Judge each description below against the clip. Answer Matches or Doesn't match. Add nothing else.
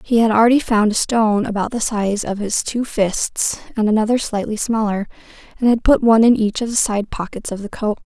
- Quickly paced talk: Matches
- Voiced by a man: Doesn't match